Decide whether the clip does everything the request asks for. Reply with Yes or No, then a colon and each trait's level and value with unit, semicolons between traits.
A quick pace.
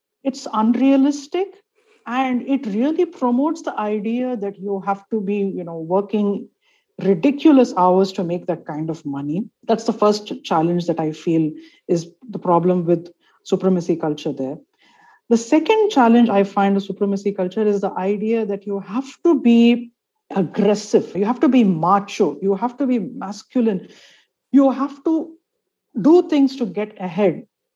No: average, 160 wpm